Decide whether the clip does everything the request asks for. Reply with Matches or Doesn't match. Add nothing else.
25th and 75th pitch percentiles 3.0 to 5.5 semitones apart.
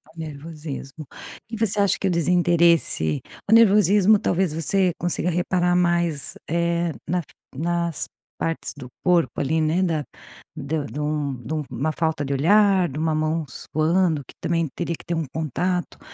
Doesn't match